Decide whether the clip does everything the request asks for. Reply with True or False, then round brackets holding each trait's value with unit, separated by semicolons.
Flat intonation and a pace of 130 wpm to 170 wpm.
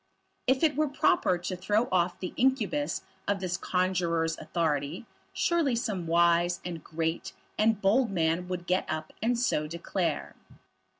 False (5.0 semitones; 145 wpm)